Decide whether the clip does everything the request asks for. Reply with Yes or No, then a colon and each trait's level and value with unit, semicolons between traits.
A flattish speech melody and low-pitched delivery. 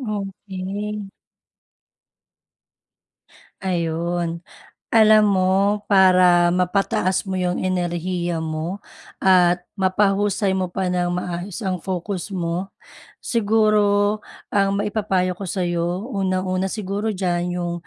No: narrow, 2.2 semitones; medium, 185 Hz